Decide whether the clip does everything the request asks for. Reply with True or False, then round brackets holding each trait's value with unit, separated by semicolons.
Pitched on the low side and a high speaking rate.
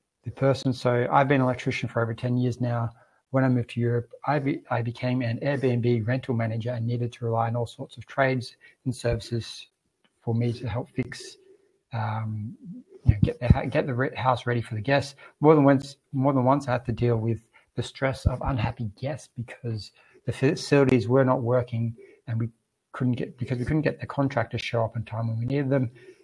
True (125 Hz; 215 wpm)